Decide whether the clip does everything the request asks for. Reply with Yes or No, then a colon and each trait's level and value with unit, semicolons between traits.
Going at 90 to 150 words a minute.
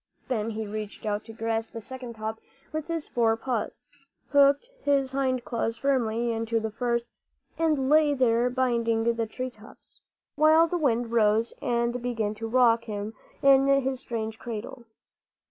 No: average, 165 wpm